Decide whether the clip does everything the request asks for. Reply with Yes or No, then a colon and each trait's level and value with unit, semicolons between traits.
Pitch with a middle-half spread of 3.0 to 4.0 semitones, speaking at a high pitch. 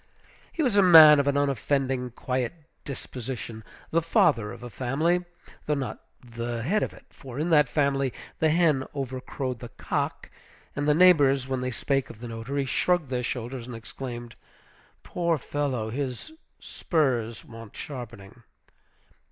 No: average, 3.6 semitones; low, 135 Hz